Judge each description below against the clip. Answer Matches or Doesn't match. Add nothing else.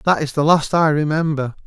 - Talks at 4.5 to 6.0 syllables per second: Matches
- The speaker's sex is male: Matches